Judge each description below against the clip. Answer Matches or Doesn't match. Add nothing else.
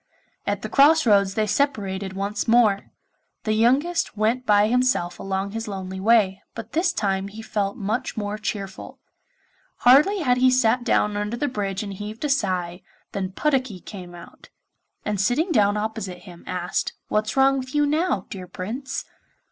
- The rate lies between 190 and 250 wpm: Doesn't match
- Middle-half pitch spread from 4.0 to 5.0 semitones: Matches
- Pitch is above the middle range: Matches